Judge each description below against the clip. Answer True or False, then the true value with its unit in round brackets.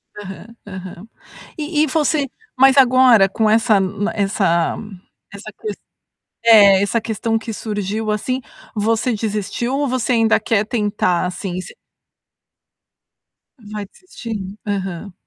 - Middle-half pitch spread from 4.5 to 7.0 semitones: False (2.8 semitones)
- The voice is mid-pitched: False (215 Hz)